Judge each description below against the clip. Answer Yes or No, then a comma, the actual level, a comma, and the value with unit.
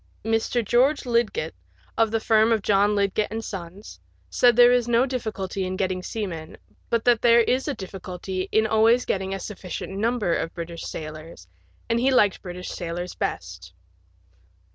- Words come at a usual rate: Yes, average, 165 wpm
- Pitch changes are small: No, average, 4.2 semitones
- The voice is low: No, high, 210 Hz